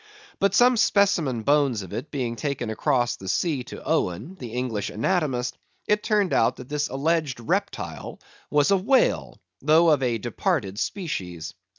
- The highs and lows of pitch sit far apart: Yes, wide, 6.3 semitones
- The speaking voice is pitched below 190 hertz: Yes, low, 135 Hz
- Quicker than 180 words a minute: No, average, 160 wpm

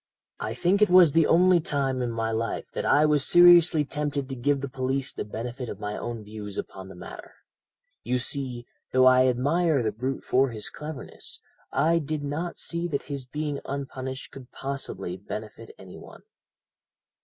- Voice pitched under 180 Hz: Yes, low, 135 Hz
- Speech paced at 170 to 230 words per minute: Yes, average, 180 wpm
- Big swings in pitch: No, average, 3.9 semitones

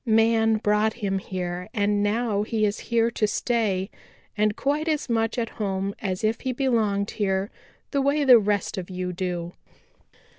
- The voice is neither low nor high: No, high, 210 Hz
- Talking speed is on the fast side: No, average, 170 wpm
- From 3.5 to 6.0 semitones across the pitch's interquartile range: No, average, 3.1 semitones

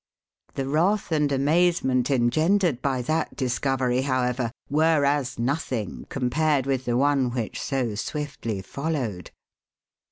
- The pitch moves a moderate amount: Yes, average, 3.4 semitones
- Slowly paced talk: Yes, slow, 120 wpm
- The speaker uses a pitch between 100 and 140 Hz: Yes, low, 135 Hz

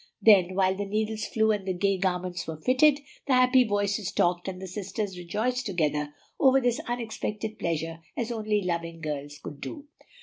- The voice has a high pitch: Yes, high, 200 Hz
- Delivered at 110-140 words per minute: No, average, 175 wpm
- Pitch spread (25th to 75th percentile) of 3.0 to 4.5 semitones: Yes, average, 4.0 semitones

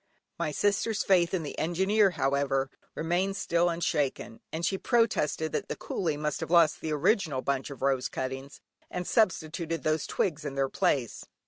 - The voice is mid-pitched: Yes, medium, 160 Hz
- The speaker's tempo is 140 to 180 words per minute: Yes, average, 165 wpm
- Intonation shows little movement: No, average, 4.4 semitones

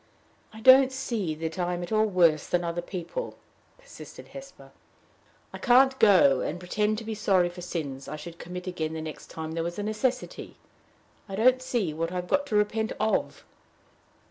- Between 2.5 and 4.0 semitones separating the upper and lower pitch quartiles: No, average, 4.9 semitones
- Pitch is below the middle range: No, medium, 185 Hz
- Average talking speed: Yes, average, 180 wpm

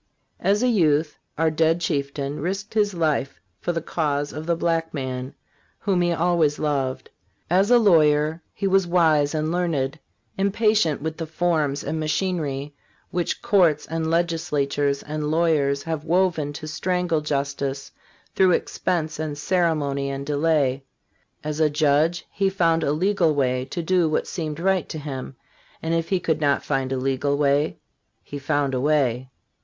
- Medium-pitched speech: Yes, medium, 155 Hz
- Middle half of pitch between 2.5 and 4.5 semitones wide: Yes, average, 3.2 semitones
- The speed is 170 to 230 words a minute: No, average, 160 wpm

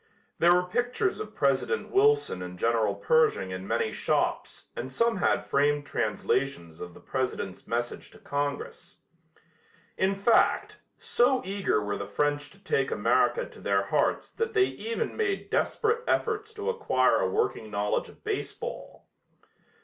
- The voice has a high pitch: No, medium, 160 Hz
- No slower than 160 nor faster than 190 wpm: No, average, 150 wpm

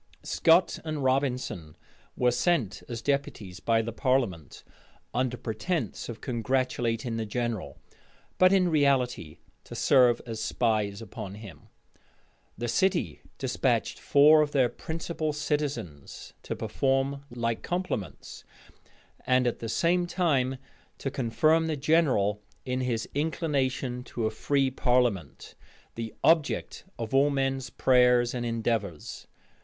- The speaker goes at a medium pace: No, slow, 125 wpm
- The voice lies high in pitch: No, low, 125 Hz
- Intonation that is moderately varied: Yes, average, 4.1 semitones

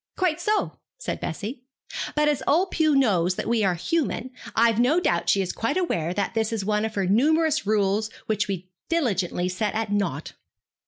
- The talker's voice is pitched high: Yes, high, 220 Hz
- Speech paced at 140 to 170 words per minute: No, average, 190 wpm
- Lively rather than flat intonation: Yes, wide, 7.4 semitones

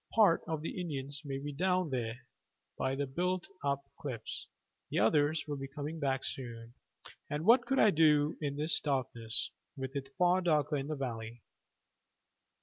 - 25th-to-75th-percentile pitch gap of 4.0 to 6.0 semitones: No, average, 3.4 semitones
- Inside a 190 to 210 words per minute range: No, average, 165 wpm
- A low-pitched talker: No, medium, 145 Hz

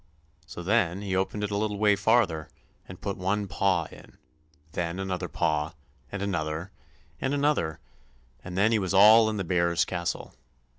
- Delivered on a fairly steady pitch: No, average, 3.2 semitones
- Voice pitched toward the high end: No, very low, 95 Hz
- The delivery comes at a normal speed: Yes, average, 170 wpm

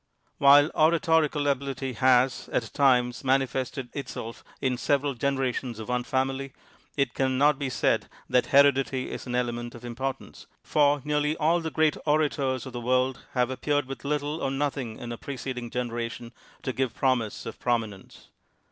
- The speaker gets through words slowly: No, average, 165 wpm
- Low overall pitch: Yes, low, 130 Hz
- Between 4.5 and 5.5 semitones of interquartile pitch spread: No, narrow, 2.5 semitones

